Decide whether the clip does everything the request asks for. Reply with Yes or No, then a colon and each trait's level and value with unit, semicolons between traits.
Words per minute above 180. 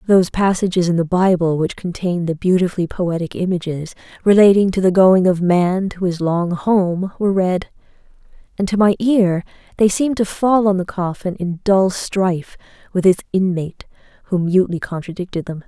No: average, 170 wpm